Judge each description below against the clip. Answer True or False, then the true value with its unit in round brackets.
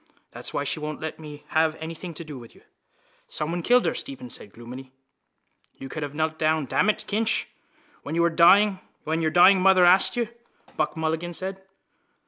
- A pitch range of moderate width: True (3.6 semitones)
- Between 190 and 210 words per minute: False (170 wpm)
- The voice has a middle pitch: True (160 Hz)